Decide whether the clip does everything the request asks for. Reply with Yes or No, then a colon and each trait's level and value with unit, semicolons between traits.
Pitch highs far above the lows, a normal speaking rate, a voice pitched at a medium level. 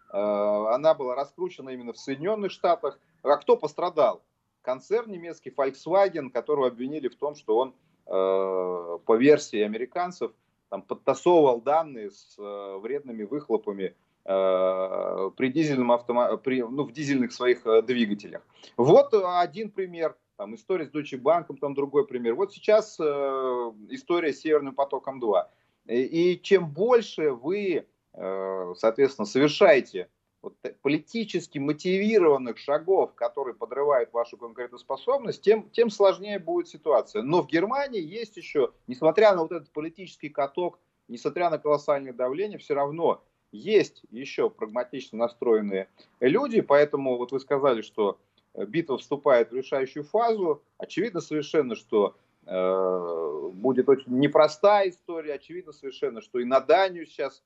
Yes: wide, 7.7 semitones; average, 125 wpm; medium, 150 Hz